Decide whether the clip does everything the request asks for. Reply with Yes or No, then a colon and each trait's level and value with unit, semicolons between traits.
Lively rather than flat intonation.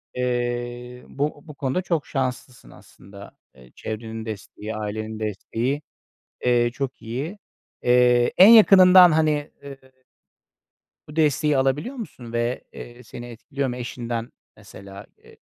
No: average, 4.2 semitones